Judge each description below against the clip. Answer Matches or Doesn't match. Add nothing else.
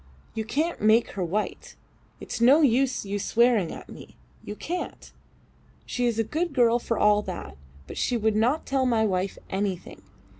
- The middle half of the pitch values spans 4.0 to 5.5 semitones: Doesn't match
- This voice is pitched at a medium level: Doesn't match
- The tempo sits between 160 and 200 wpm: Matches